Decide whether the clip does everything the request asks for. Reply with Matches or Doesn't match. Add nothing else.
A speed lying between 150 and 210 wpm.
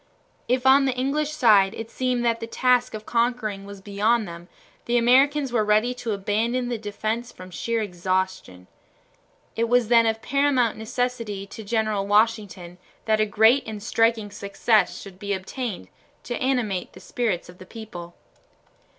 Matches